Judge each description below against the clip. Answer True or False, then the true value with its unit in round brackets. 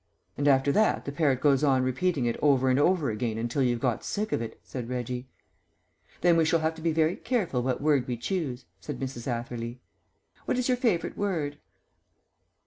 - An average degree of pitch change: True (4.9 semitones)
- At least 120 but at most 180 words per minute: False (195 wpm)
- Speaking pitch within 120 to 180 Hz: True (140 Hz)